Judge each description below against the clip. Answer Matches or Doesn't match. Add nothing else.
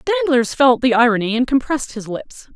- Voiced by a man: Doesn't match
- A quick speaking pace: Doesn't match